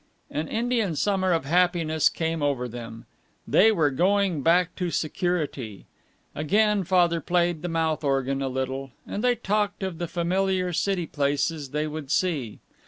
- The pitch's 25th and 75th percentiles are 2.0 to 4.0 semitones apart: No, average, 4.5 semitones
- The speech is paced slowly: No, average, 155 wpm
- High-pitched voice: No, medium, 165 Hz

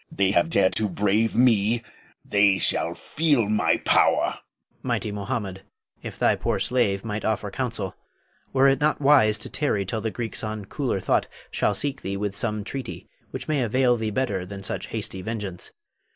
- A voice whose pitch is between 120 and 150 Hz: No, low, 110 Hz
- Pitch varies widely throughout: No, average, 3.8 semitones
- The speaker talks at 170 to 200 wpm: Yes, average, 180 wpm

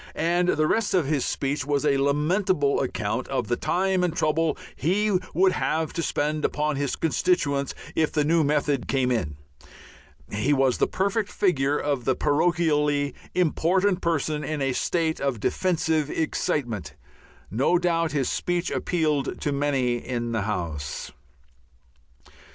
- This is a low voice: No, medium, 150 Hz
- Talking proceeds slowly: No, average, 145 wpm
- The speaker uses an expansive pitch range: No, average, 3.8 semitones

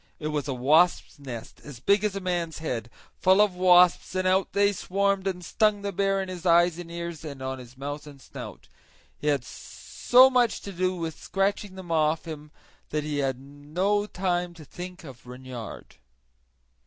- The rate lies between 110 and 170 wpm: No, average, 190 wpm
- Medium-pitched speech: Yes, medium, 170 Hz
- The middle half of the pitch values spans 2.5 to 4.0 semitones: No, average, 4.8 semitones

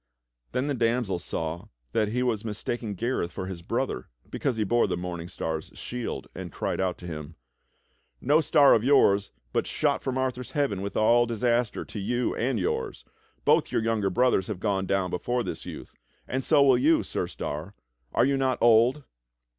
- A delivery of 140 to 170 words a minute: No, average, 185 wpm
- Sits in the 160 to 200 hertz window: No, low, 115 Hz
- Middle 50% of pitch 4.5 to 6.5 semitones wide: Yes, average, 4.8 semitones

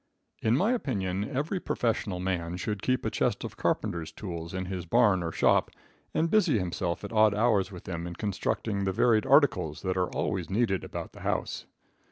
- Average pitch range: Yes, average, 4.7 semitones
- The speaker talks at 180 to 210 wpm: Yes, average, 190 wpm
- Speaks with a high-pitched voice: No, low, 100 Hz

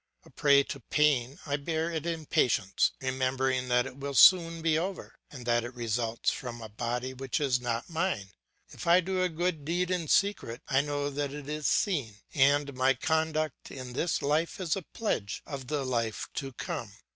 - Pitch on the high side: No, medium, 140 Hz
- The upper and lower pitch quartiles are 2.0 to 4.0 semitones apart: No, average, 4.4 semitones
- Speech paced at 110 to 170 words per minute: No, average, 190 wpm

